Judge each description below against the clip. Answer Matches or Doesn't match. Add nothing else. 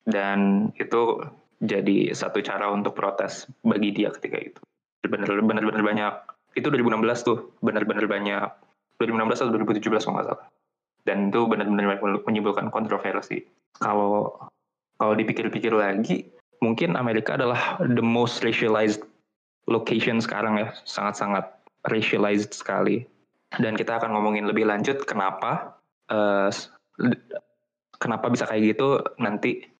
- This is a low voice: Matches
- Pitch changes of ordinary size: Doesn't match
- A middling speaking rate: Matches